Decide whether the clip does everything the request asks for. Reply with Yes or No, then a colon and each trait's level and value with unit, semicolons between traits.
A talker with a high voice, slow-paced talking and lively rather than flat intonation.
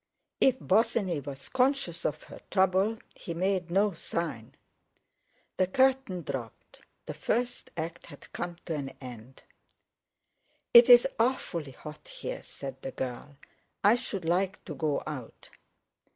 No: medium, 175 Hz; slow, 130 wpm; wide, 6.8 semitones